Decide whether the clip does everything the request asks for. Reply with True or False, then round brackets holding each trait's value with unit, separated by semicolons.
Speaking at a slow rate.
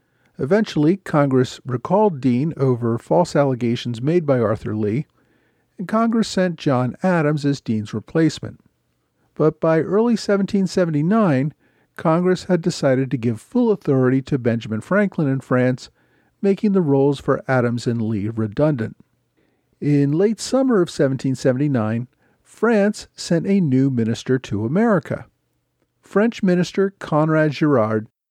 True (125 wpm)